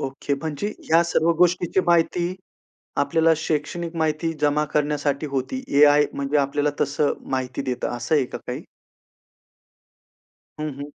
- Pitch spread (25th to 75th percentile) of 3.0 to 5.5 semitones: No, narrow, 2.5 semitones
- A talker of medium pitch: Yes, medium, 150 Hz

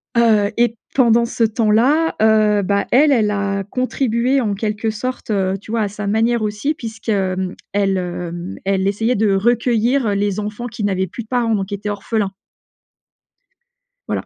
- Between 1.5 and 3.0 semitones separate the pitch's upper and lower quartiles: Yes, average, 2.7 semitones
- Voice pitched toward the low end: No, high, 215 Hz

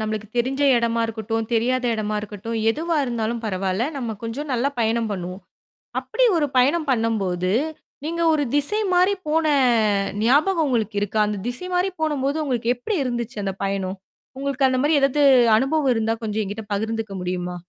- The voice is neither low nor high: No, high, 235 Hz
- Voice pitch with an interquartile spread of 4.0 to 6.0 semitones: Yes, average, 4.6 semitones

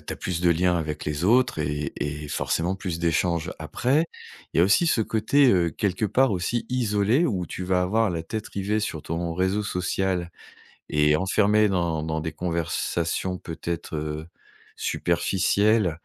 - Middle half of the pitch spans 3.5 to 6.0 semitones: Yes, average, 4.1 semitones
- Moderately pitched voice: No, very low, 90 Hz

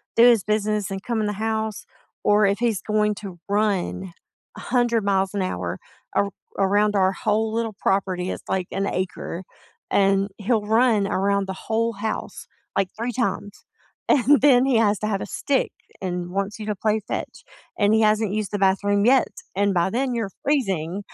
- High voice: Yes, high, 205 Hz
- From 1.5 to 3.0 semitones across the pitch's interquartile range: Yes, narrow, 2.4 semitones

